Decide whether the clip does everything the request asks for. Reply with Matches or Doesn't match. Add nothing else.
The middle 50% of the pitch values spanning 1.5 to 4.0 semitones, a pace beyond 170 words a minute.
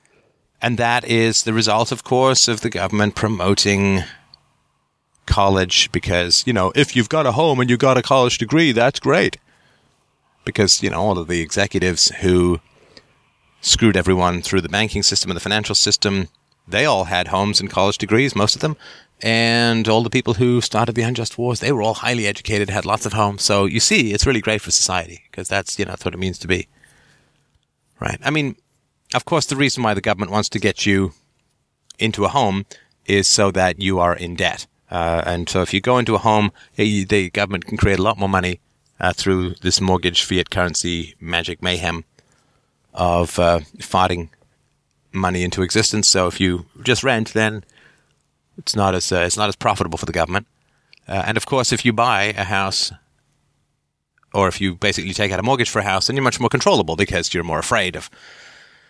Matches